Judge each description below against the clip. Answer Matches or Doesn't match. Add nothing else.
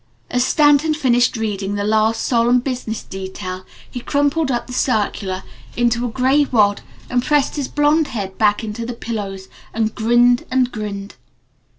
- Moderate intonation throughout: Matches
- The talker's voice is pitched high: Matches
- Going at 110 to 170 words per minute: Matches